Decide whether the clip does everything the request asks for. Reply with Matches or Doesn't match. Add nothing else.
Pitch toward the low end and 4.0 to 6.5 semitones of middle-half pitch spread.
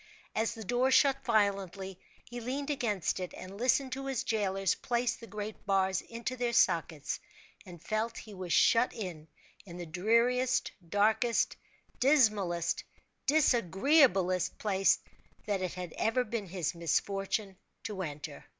Doesn't match